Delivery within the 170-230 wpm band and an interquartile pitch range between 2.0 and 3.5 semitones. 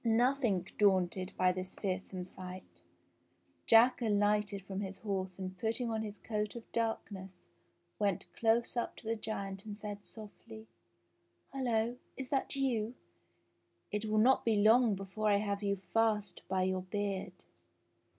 No: average, 150 wpm; average, 2.8 semitones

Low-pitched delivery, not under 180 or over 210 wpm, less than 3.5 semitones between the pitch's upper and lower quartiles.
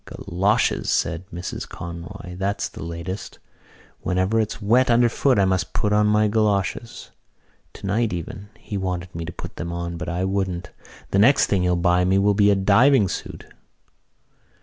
No: very low, 95 Hz; average, 165 wpm; average, 3.0 semitones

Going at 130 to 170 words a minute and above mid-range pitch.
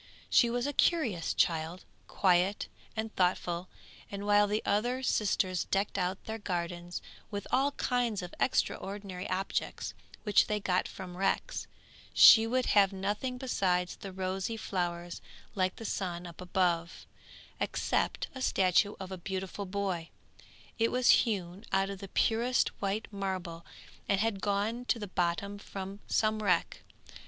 Yes: average, 145 wpm; high, 195 Hz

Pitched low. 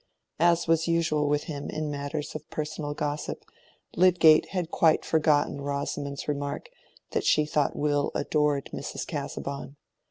No: medium, 150 Hz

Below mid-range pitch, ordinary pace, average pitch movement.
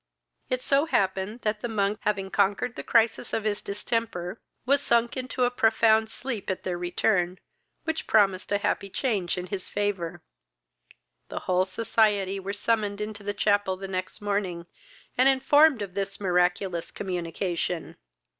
No: high, 205 Hz; average, 155 wpm; average, 3.2 semitones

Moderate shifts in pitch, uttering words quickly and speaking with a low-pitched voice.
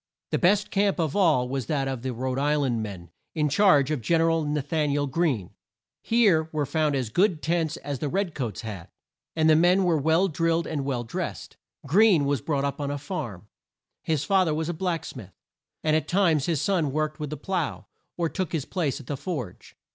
No: average, 3.8 semitones; fast, 225 wpm; medium, 155 Hz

